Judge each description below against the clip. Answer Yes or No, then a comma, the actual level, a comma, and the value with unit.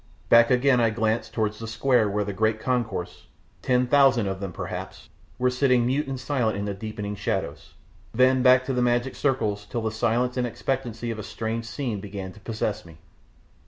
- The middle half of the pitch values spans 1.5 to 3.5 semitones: Yes, average, 3.2 semitones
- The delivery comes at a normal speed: Yes, average, 195 wpm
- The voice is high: No, low, 115 Hz